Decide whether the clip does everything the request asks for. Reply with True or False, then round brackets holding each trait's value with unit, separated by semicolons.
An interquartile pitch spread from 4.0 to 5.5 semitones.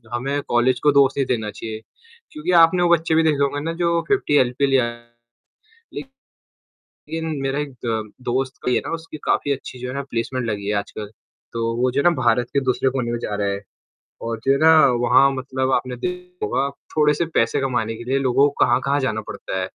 False (3.6 semitones)